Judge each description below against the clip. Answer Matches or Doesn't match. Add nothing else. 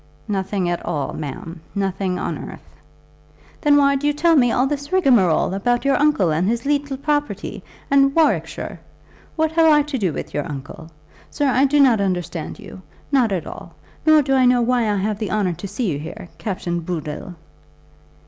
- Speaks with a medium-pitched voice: Doesn't match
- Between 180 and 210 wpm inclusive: Matches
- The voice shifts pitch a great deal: Matches